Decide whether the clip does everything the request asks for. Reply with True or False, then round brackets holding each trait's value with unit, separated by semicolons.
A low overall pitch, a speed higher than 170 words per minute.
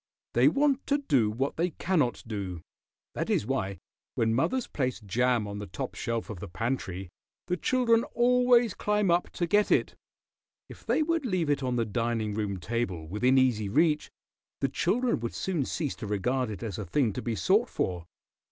True (125 Hz; 190 wpm)